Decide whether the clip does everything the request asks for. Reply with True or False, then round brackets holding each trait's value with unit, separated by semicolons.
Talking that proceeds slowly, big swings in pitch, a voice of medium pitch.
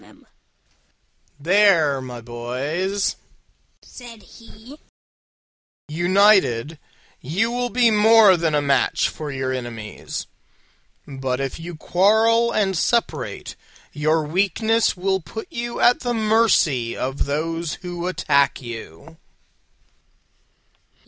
True (100 wpm; 7.6 semitones; 175 Hz)